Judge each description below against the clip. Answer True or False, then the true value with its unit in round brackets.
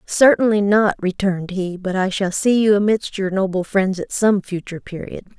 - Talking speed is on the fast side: False (190 wpm)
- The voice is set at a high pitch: True (195 Hz)